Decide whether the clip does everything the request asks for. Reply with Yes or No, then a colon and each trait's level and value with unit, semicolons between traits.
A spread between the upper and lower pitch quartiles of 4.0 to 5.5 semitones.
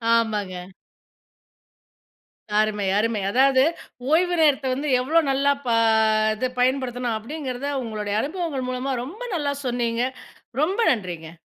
Yes: average, 4.3 semitones